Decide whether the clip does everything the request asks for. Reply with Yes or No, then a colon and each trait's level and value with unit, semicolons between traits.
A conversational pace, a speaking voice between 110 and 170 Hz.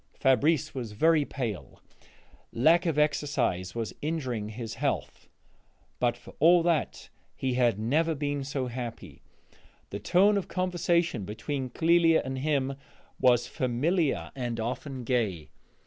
No: slow, 130 wpm; low, 135 Hz